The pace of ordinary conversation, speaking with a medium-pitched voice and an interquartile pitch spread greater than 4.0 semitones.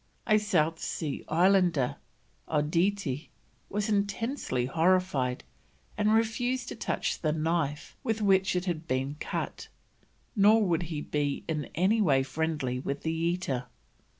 No: slow, 130 wpm; medium, 165 Hz; average, 5.3 semitones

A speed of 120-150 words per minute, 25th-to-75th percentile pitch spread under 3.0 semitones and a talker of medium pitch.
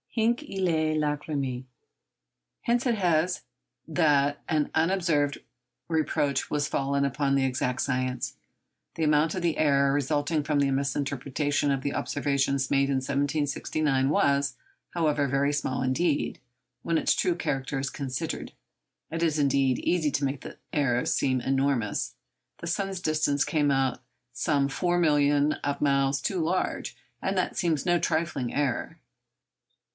Yes: average, 140 wpm; narrow, 2.6 semitones; medium, 145 Hz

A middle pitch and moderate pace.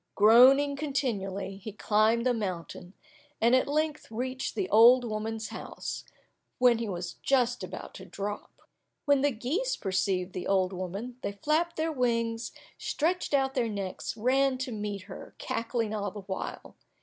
No: high, 230 Hz; average, 155 wpm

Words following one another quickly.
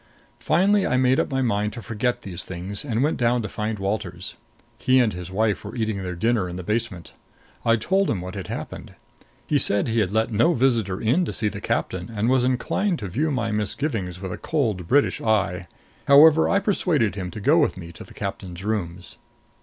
Yes: fast, 210 wpm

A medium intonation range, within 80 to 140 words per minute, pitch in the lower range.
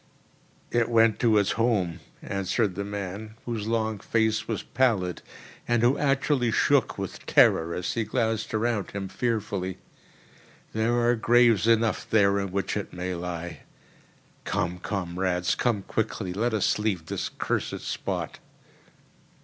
Yes: average, 3.5 semitones; slow, 135 wpm; low, 110 Hz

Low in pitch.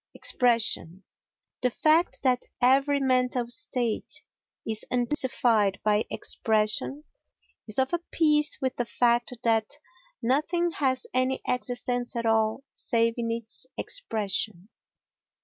No: high, 245 Hz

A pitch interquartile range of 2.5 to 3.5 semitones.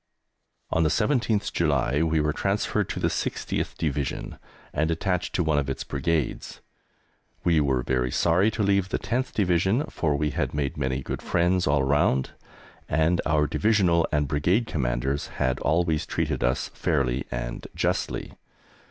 No: average, 4.4 semitones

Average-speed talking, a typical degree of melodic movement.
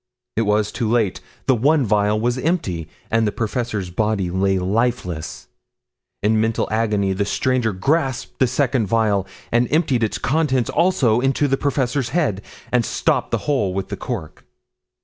Yes: average, 160 wpm; average, 4.2 semitones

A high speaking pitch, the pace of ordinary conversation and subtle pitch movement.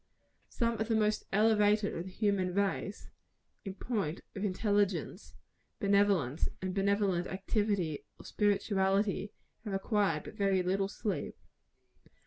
No: high, 200 Hz; slow, 120 wpm; narrow, 1.7 semitones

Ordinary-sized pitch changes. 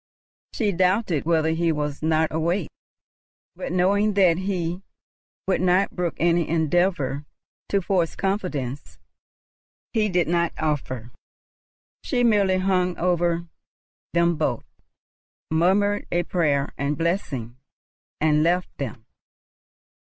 Yes: average, 3.0 semitones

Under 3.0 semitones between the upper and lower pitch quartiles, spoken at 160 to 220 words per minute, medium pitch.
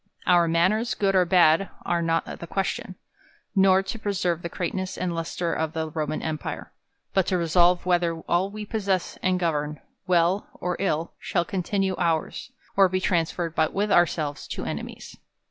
Yes: narrow, 2.4 semitones; average, 165 wpm; medium, 175 Hz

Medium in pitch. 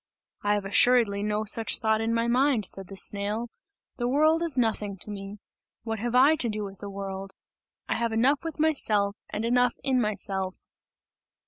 No: high, 220 Hz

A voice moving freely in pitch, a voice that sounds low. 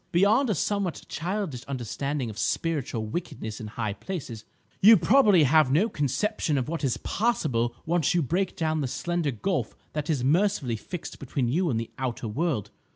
No: wide, 6.4 semitones; medium, 150 Hz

